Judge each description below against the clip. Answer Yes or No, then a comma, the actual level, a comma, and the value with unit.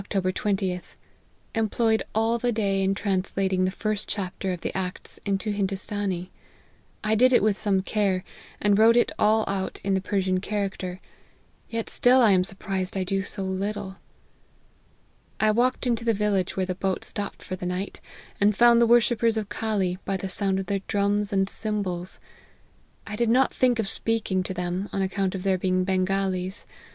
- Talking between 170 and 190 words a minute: Yes, average, 180 wpm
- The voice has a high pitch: Yes, high, 195 Hz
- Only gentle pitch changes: Yes, narrow, 2.3 semitones